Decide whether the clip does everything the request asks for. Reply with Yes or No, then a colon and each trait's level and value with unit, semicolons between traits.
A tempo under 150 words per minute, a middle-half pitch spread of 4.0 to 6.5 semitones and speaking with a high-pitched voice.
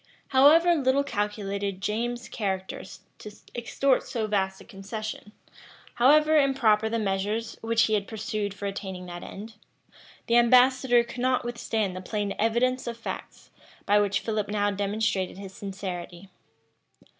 No: average, 140 wpm; average, 3.3 semitones; high, 215 Hz